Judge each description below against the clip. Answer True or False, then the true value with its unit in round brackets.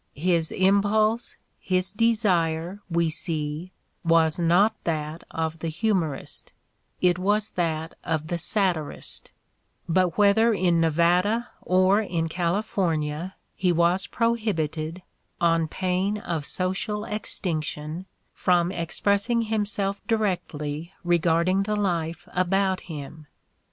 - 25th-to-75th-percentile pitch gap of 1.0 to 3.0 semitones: False (3.6 semitones)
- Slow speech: True (110 wpm)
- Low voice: False (180 Hz)